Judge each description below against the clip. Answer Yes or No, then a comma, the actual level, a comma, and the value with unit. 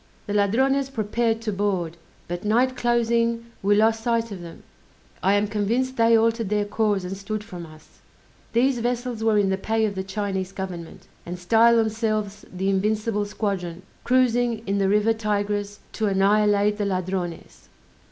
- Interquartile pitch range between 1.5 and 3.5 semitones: Yes, average, 2.7 semitones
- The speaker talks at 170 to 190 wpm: No, average, 160 wpm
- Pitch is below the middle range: No, high, 210 Hz